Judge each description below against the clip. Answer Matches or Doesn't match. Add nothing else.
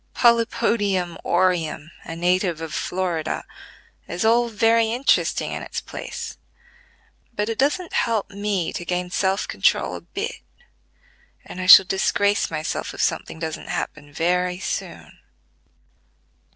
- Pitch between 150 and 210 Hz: Matches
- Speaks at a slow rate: Matches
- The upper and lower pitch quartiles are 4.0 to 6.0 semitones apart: Matches